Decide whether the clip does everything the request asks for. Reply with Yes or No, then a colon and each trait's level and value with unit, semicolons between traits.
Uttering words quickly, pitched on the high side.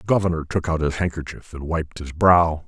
No: fast, 225 wpm; very low, 80 Hz